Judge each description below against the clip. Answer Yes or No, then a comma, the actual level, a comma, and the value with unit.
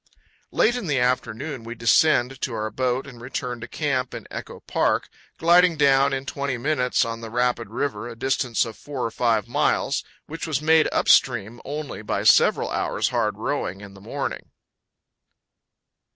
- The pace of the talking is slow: No, average, 170 wpm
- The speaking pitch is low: Yes, low, 125 Hz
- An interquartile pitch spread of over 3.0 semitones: Yes, average, 3.6 semitones